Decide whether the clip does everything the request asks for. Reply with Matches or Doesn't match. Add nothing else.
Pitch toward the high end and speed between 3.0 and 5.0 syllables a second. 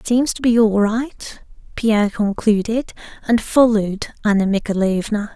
Matches